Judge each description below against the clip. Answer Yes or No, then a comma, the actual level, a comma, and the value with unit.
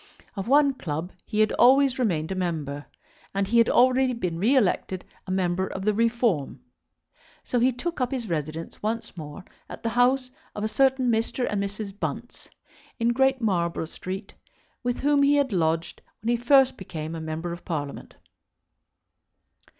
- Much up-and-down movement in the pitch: Yes, wide, 6.4 semitones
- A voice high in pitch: Yes, high, 215 Hz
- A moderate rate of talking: Yes, average, 170 wpm